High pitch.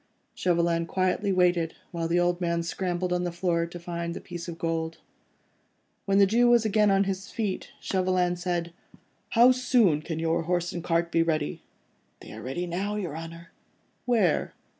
No: medium, 175 Hz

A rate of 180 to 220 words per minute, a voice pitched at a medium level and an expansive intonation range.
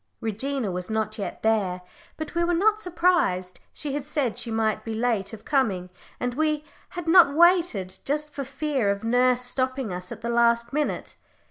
No: average, 185 wpm; high, 245 Hz; wide, 5.7 semitones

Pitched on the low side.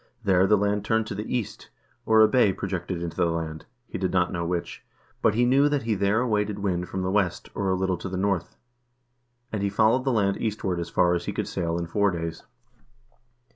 Yes: very low, 95 Hz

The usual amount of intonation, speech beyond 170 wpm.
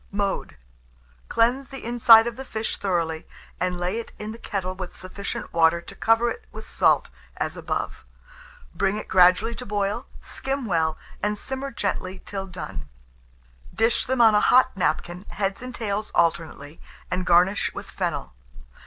No: average, 4.1 semitones; average, 160 wpm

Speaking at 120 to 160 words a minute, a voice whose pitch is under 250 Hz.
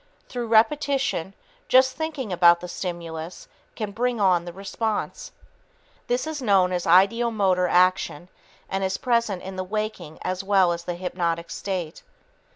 Yes: average, 145 wpm; high, 190 Hz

